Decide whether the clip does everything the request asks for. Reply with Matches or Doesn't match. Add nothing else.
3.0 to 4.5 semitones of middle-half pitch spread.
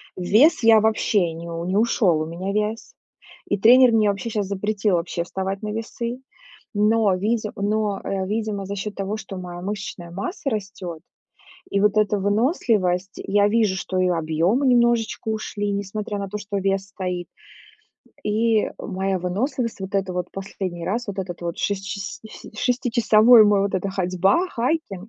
Doesn't match